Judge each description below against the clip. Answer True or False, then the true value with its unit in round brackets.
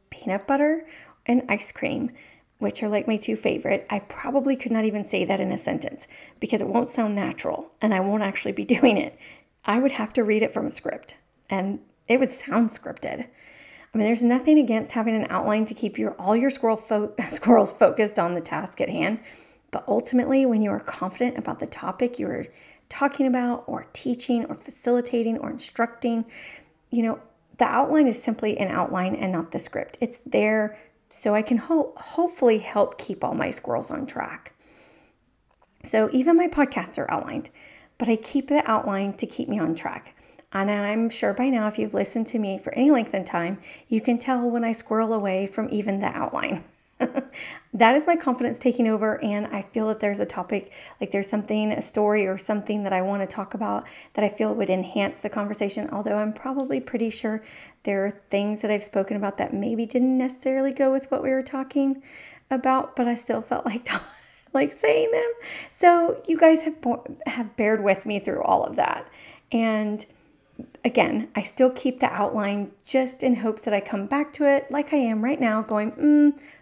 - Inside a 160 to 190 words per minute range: False (200 wpm)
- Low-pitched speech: False (230 Hz)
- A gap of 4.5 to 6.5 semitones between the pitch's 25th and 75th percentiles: False (4.0 semitones)